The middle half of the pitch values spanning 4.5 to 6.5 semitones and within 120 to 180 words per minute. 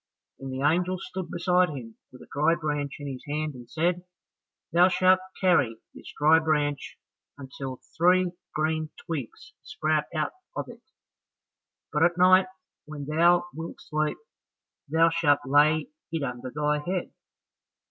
No: average, 3.2 semitones; average, 145 wpm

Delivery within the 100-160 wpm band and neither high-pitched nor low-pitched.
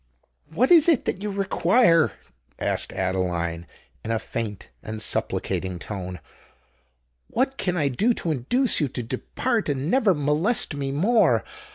Yes: average, 145 wpm; medium, 150 Hz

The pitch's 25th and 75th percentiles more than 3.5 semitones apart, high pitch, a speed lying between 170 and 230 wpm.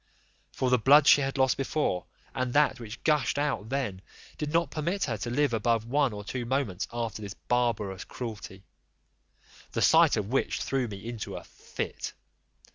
No: average, 4.4 semitones; low, 125 Hz; average, 175 wpm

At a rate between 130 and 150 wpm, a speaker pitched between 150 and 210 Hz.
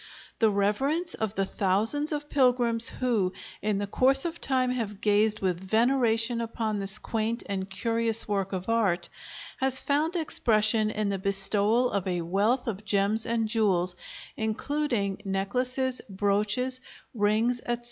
No: average, 145 wpm; high, 220 Hz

